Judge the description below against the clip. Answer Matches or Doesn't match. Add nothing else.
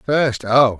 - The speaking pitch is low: Matches